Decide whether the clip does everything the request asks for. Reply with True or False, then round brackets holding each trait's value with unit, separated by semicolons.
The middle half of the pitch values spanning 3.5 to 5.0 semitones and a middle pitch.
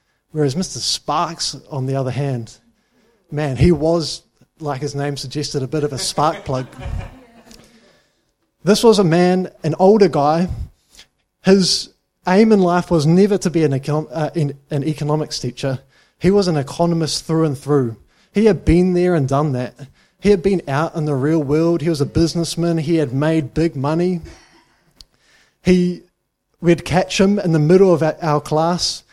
True (3.8 semitones; 160 Hz)